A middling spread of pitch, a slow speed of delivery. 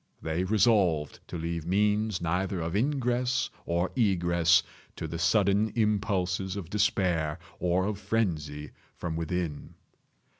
Yes: average, 4.0 semitones; slow, 120 wpm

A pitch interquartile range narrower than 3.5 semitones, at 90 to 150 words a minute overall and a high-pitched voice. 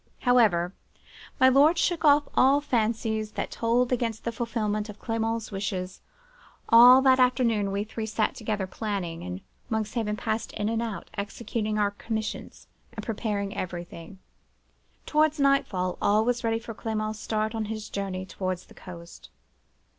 Yes: average, 2.7 semitones; average, 145 wpm; high, 220 Hz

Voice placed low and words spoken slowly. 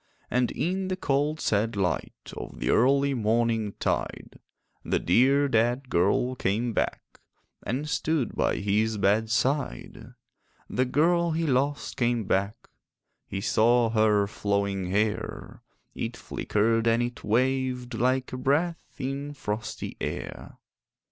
Yes: low, 120 Hz; slow, 120 wpm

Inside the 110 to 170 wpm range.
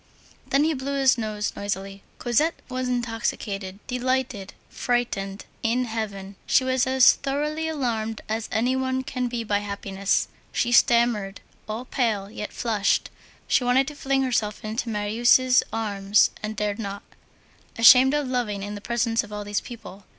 Yes: average, 155 wpm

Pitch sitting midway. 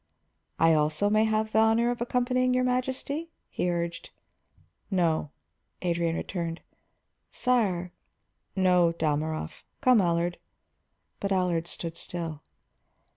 Yes: medium, 180 Hz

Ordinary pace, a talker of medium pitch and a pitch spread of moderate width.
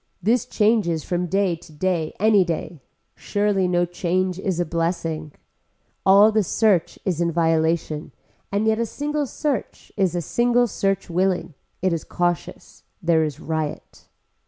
Yes: average, 150 wpm; medium, 180 Hz; average, 3.7 semitones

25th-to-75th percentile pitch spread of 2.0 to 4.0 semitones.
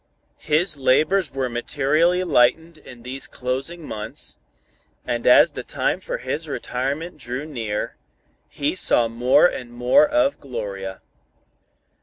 No: average, 5.1 semitones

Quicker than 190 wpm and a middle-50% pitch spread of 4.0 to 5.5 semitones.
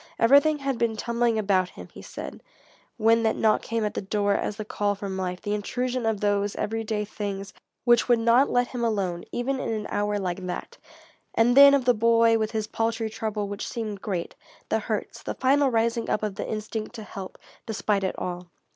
No: fast, 205 wpm; narrow, 2.4 semitones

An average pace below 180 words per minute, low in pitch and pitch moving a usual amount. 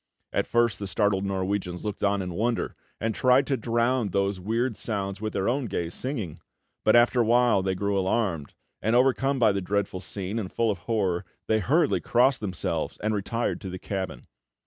No: average, 190 wpm; low, 105 Hz; average, 3.6 semitones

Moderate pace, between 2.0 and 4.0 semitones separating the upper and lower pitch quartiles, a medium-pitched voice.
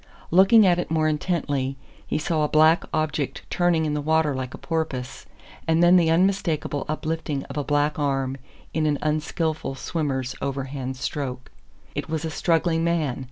Yes: average, 165 wpm; average, 2.8 semitones; medium, 155 Hz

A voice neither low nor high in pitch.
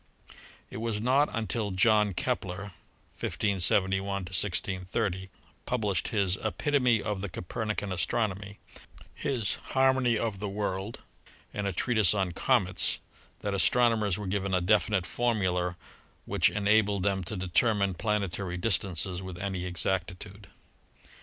No: low, 100 Hz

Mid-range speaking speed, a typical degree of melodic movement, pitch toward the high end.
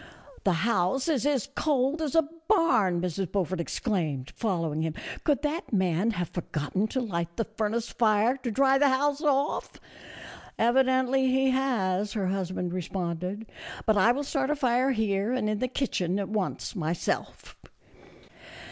No: average, 165 wpm; wide, 6.3 semitones; high, 220 Hz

